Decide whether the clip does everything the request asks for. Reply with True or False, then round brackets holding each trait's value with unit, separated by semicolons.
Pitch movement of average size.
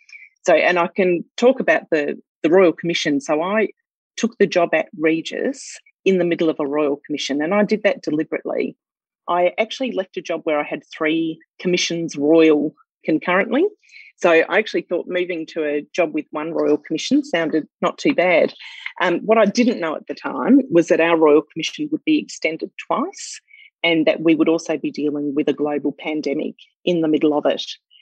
False (6.1 semitones)